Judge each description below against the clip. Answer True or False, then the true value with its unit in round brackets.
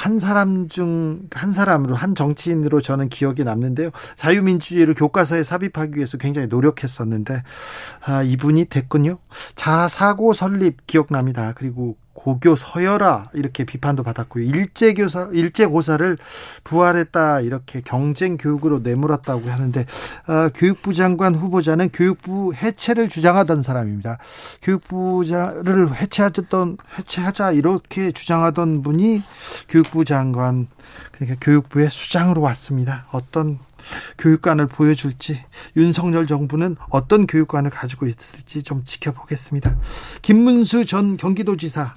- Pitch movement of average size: True (4.9 semitones)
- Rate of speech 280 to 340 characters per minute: True (325 characters per minute)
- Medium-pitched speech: True (155 Hz)